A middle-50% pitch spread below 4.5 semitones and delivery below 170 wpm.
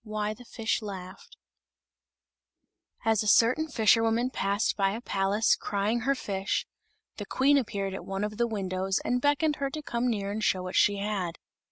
No: average, 3.6 semitones; average, 175 wpm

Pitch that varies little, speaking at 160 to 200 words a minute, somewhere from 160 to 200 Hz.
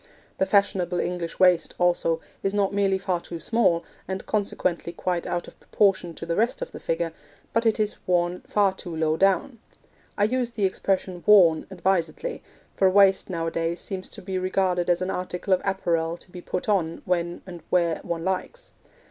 Yes: narrow, 2.3 semitones; average, 185 wpm; medium, 185 Hz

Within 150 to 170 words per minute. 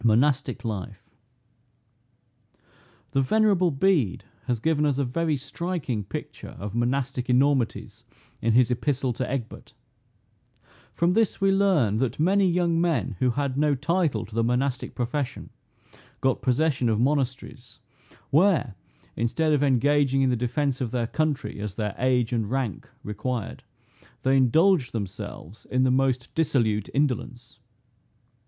No: slow, 135 wpm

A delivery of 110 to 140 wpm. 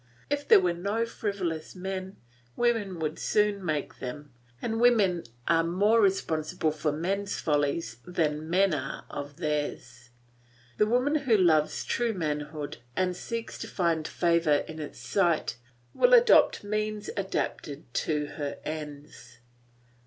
Yes: slow, 135 wpm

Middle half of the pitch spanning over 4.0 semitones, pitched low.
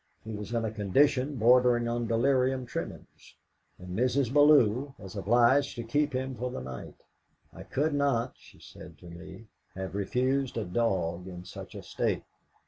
Yes: average, 4.6 semitones; low, 120 Hz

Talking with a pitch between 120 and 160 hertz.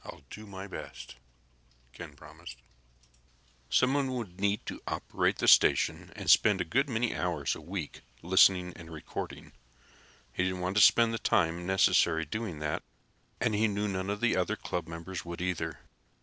No: very low, 95 Hz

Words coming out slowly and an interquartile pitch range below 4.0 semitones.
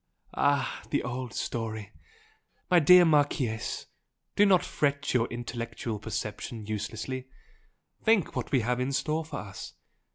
No: slow, 130 wpm; average, 4.4 semitones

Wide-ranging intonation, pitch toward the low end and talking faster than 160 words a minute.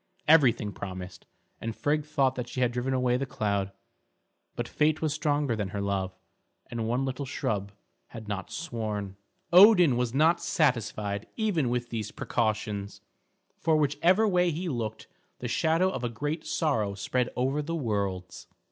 No: wide, 6.2 semitones; low, 125 Hz; average, 155 wpm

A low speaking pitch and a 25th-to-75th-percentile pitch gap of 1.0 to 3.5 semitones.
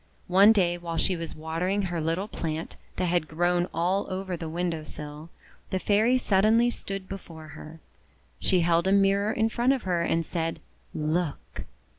No: medium, 175 Hz; average, 3.0 semitones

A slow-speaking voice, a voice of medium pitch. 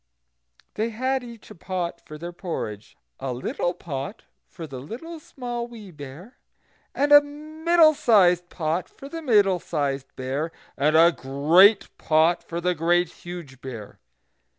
No: average, 150 wpm; medium, 175 Hz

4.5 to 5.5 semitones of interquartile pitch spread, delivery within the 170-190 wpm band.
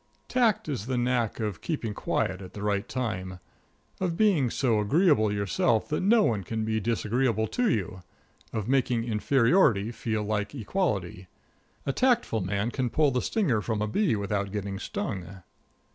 No: average, 5.1 semitones; average, 160 wpm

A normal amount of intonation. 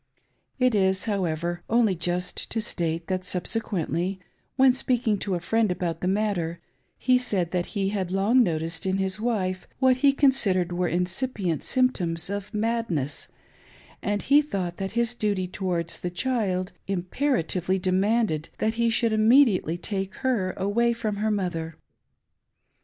Yes: average, 4.3 semitones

